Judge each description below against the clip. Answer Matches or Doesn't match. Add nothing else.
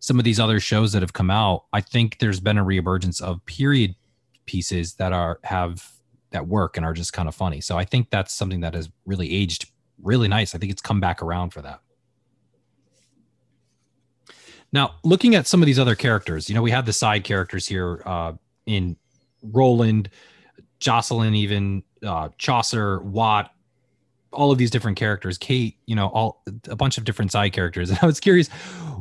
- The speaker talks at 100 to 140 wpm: Doesn't match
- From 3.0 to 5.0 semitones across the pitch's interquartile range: Matches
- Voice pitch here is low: Matches